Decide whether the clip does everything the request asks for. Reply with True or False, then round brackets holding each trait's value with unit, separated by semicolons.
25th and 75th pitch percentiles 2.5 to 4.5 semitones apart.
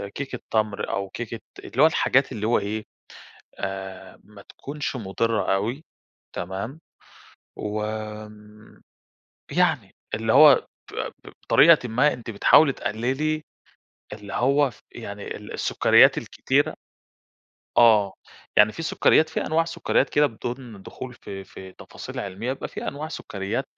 False (5.3 semitones)